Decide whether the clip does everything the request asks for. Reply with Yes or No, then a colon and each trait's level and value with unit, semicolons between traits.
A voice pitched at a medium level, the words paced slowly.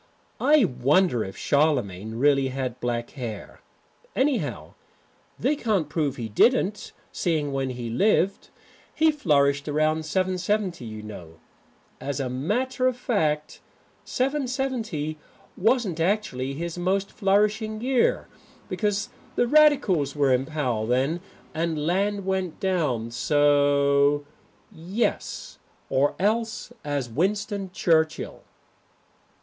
Yes: medium, 160 Hz; slow, 115 wpm